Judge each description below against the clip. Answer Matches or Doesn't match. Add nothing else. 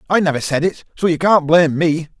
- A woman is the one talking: Doesn't match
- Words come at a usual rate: Doesn't match